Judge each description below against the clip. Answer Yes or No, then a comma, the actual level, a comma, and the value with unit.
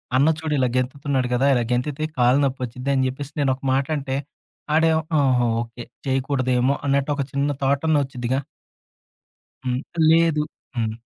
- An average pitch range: No, narrow, 2.1 semitones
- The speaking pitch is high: No, low, 135 Hz